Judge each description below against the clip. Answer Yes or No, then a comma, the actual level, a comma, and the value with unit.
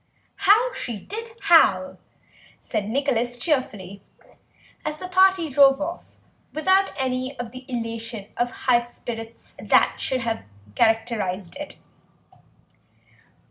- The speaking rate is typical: No, slow, 110 wpm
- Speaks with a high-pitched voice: Yes, very high, 250 Hz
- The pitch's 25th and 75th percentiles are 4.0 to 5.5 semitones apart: Yes, average, 5.2 semitones